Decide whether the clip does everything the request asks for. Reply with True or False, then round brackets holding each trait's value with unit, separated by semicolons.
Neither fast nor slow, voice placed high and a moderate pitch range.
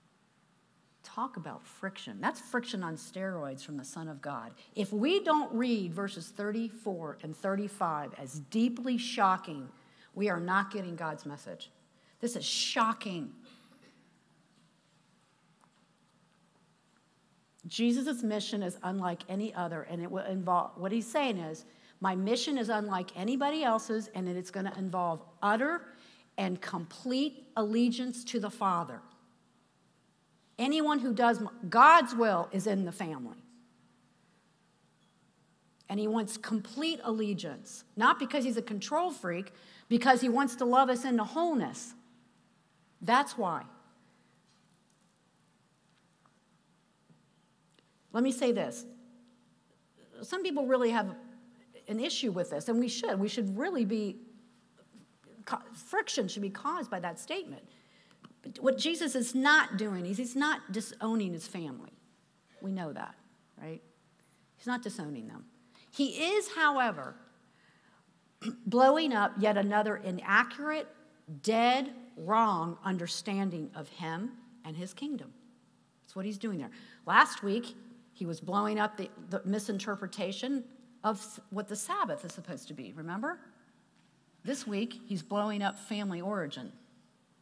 False (130 wpm; 220 Hz; 4.5 semitones)